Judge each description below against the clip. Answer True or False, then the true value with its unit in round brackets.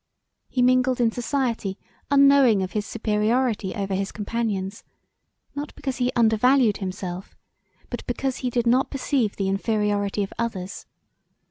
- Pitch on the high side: True (225 Hz)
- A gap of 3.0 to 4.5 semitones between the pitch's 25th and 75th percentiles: True (4.1 semitones)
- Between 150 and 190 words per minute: False (135 wpm)